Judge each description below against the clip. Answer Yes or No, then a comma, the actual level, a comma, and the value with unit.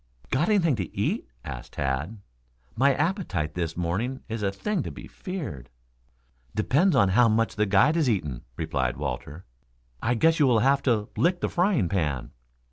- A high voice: No, low, 110 Hz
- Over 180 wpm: No, average, 170 wpm